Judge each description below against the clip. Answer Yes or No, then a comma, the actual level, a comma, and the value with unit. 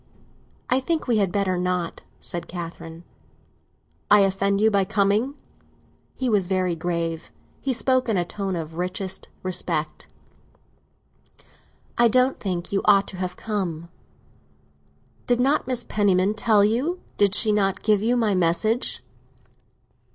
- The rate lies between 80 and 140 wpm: Yes, slow, 135 wpm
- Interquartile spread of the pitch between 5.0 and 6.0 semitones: No, average, 3.7 semitones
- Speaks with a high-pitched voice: Yes, high, 200 Hz